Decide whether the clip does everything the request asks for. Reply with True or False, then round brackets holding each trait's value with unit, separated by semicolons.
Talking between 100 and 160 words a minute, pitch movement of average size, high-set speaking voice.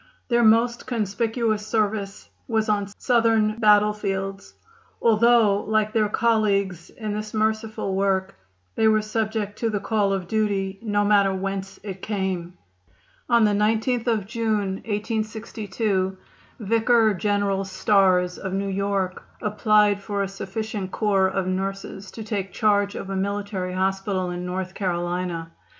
False (135 wpm; 2.1 semitones; 205 Hz)